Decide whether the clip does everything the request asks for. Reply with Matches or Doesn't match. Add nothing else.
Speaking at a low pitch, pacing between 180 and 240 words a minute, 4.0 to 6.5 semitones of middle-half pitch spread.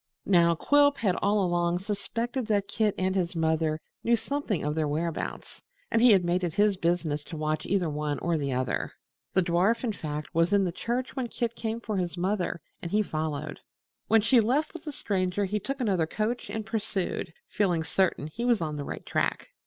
Doesn't match